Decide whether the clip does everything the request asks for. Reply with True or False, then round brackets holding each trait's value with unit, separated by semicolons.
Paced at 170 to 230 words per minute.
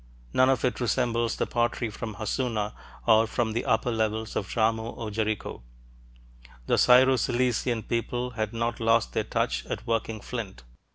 False (160 wpm)